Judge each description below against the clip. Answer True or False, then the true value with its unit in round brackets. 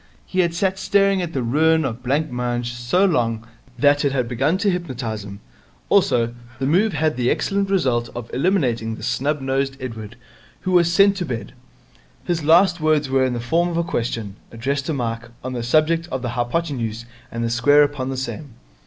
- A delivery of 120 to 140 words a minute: False (195 wpm)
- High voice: False (135 Hz)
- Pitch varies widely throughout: True (5.8 semitones)